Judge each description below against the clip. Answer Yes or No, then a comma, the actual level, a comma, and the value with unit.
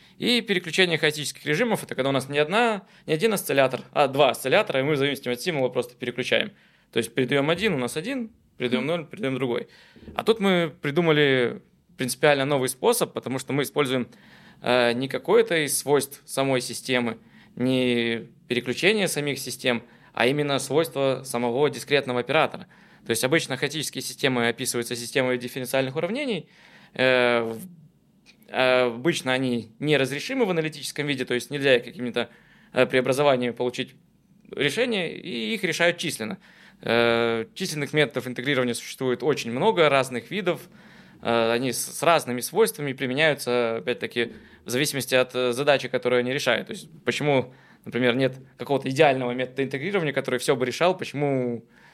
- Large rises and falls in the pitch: No, average, 4.0 semitones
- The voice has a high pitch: No, low, 135 Hz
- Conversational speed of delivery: Yes, average, 145 wpm